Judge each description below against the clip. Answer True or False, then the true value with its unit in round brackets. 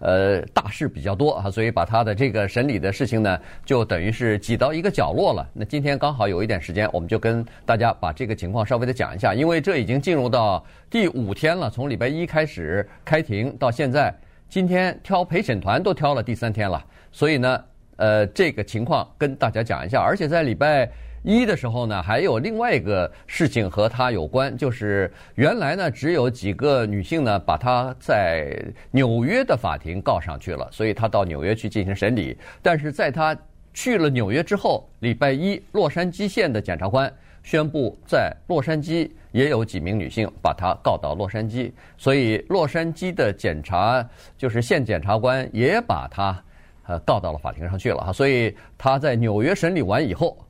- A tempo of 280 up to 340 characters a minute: True (290 characters per minute)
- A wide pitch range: True (6.0 semitones)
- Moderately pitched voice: False (120 Hz)